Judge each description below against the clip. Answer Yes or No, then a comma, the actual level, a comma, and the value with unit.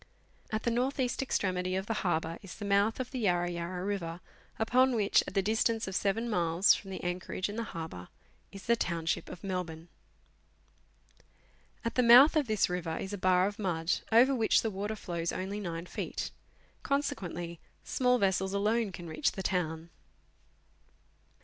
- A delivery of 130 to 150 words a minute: No, average, 175 wpm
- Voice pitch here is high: Yes, high, 195 Hz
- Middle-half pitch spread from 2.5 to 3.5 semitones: No, average, 4.3 semitones